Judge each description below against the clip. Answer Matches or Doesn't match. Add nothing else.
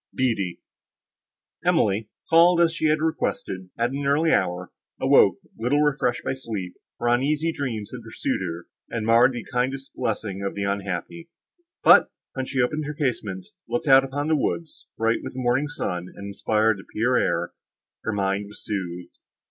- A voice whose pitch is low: Matches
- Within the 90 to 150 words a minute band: Doesn't match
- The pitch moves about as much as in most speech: Doesn't match